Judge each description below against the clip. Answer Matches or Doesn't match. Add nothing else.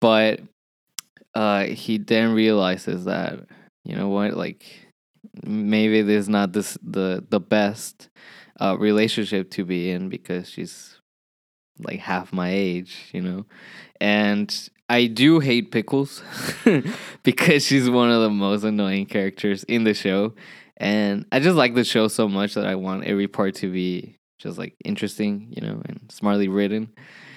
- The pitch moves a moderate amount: Doesn't match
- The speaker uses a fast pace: Doesn't match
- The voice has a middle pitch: Doesn't match